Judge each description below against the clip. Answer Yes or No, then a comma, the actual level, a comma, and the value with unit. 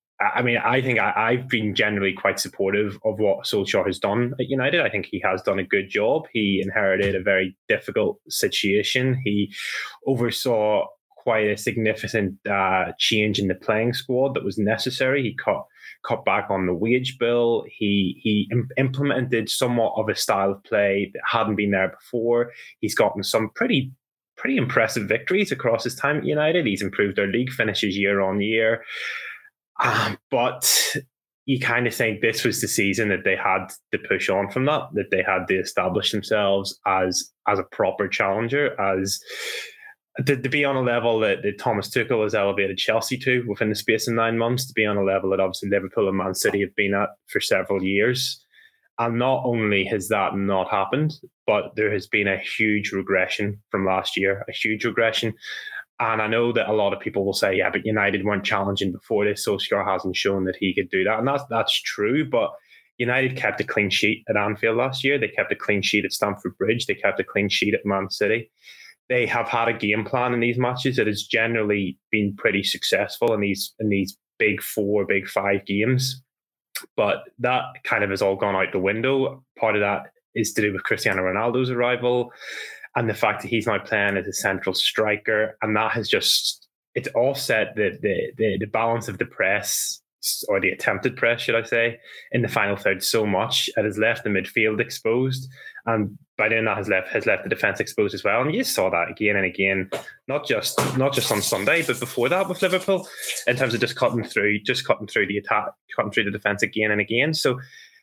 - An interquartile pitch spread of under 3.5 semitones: No, average, 4.1 semitones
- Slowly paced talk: No, fast, 205 wpm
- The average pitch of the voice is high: No, low, 110 Hz